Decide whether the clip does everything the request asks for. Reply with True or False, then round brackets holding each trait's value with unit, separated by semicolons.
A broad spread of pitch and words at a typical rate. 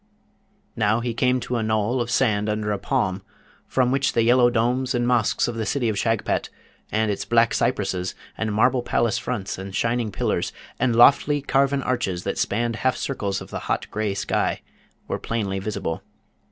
False (2.9 semitones; 180 wpm)